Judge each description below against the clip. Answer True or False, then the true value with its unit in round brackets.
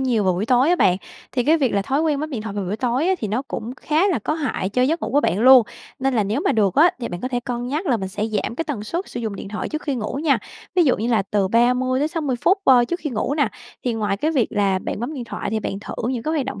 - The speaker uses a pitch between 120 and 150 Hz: False (245 Hz)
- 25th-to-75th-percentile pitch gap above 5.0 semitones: True (5.4 semitones)